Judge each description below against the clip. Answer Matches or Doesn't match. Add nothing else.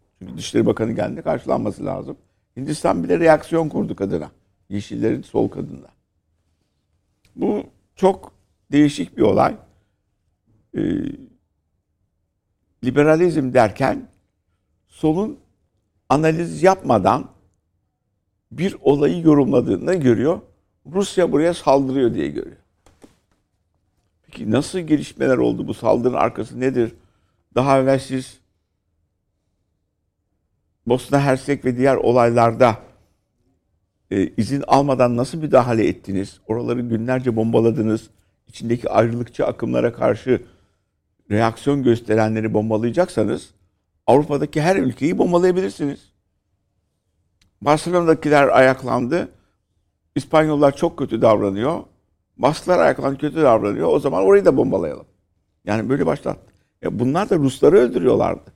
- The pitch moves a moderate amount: Doesn't match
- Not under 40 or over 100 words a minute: Matches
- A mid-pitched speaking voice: Doesn't match